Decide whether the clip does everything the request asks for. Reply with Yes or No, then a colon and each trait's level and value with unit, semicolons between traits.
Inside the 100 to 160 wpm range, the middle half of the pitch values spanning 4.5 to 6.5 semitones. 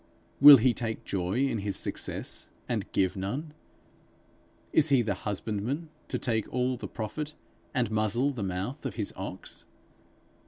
Yes: average, 150 wpm; average, 5.1 semitones